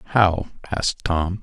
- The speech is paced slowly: Yes, slow, 125 wpm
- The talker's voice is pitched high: No, very low, 90 Hz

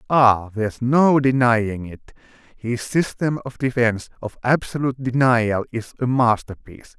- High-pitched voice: No, low, 120 Hz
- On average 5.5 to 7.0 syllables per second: No, 4.6 syllables/s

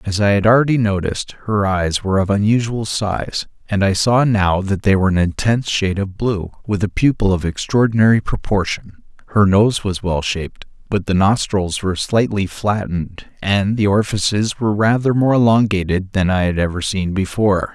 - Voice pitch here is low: Yes, low, 100 Hz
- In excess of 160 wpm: Yes, average, 180 wpm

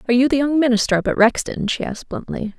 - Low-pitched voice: No, high, 245 Hz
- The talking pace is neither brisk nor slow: No, fast, 255 wpm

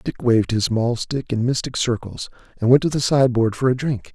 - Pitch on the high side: No, low, 120 Hz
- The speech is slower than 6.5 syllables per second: Yes, 5.6 syllables/s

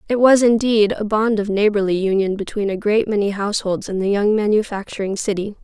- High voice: Yes, high, 205 Hz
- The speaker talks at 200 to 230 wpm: No, average, 190 wpm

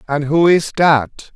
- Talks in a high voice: No, medium, 150 Hz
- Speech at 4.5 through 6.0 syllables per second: No, 3.6 syllables/s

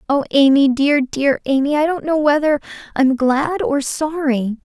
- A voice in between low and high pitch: No, very high, 285 Hz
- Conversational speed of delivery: Yes, average, 180 wpm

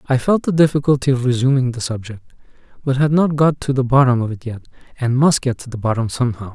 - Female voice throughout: No, male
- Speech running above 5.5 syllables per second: Yes, 6.5 syllables/s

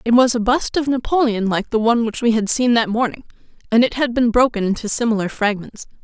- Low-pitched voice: No, high, 230 Hz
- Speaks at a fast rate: Yes, fast, 230 wpm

